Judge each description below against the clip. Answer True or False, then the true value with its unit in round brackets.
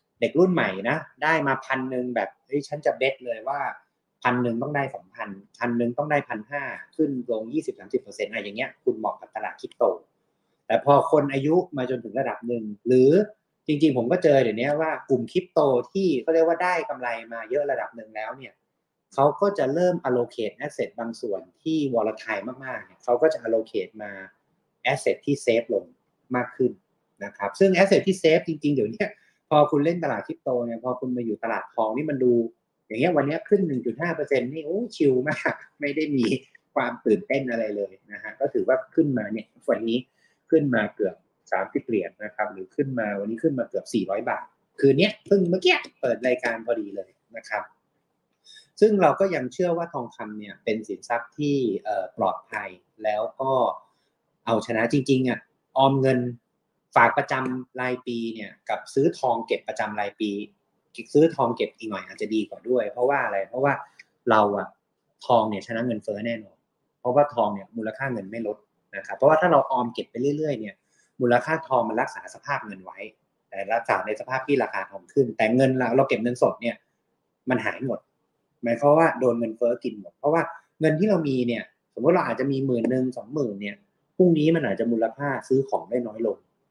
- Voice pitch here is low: True (130 Hz)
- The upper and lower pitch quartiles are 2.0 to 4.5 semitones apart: False (5.0 semitones)